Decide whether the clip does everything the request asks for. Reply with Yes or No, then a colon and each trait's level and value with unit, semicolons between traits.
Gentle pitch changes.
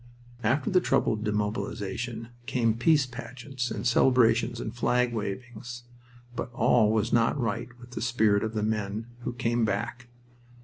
Yes: narrow, 2.1 semitones